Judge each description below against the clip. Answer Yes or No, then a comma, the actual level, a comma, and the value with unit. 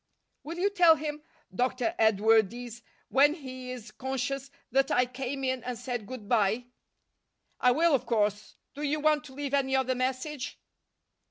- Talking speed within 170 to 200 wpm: No, average, 160 wpm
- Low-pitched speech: No, very high, 255 Hz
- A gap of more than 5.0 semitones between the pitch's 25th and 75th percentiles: No, average, 2.7 semitones